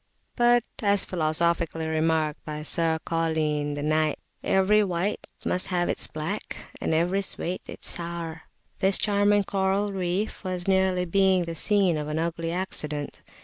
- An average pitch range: Yes, average, 3.3 semitones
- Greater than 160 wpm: No, average, 150 wpm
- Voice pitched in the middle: Yes, medium, 170 Hz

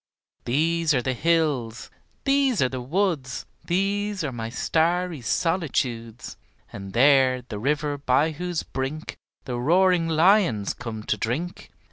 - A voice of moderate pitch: Yes, medium, 150 Hz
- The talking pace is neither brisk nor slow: No, slow, 130 wpm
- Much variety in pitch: Yes, wide, 5.8 semitones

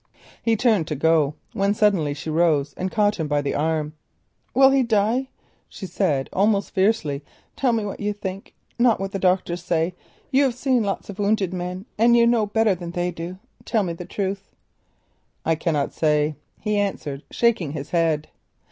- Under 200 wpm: Yes, average, 175 wpm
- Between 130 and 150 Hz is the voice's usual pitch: No, high, 190 Hz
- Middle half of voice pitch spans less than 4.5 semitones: No, average, 4.9 semitones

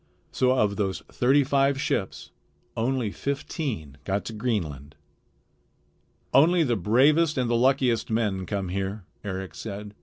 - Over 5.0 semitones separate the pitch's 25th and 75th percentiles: Yes, wide, 5.4 semitones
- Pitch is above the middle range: No, low, 115 Hz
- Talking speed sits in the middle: No, slow, 130 wpm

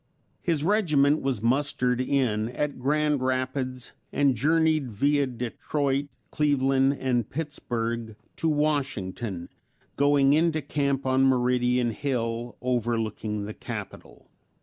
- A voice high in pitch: No, low, 130 Hz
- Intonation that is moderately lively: Yes, average, 3.1 semitones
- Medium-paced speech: No, slow, 105 wpm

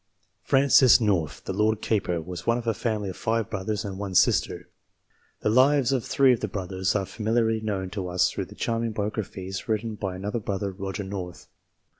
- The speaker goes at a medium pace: Yes, average, 190 wpm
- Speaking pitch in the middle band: No, low, 105 Hz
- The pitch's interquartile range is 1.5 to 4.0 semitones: Yes, average, 3.2 semitones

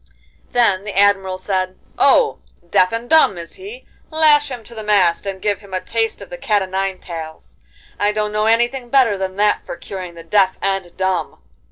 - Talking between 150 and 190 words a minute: No, average, 200 wpm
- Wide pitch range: No, average, 3.5 semitones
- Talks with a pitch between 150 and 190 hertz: No, high, 200 Hz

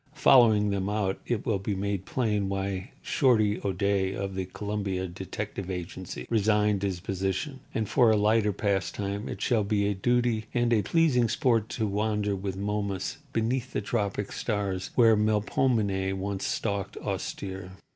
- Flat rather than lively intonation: Yes, narrow, 2.3 semitones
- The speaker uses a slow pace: No, average, 155 wpm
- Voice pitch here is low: Yes, low, 100 Hz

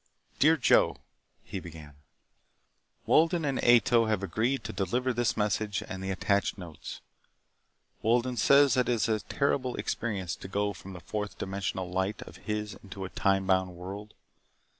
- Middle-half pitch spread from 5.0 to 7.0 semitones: No, average, 4.1 semitones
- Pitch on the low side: Yes, low, 105 Hz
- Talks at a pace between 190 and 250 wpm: No, average, 160 wpm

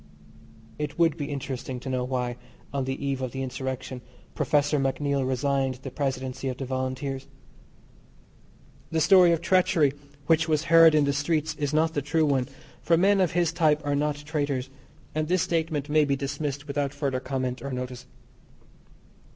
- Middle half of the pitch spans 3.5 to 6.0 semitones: No, average, 2.8 semitones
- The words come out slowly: No, average, 170 wpm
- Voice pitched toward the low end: No, medium, 145 Hz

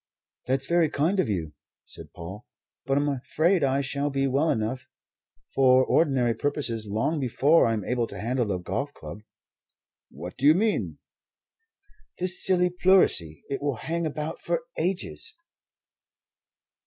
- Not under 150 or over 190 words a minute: No, average, 140 wpm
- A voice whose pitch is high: No, medium, 140 Hz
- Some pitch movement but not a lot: No, wide, 5.7 semitones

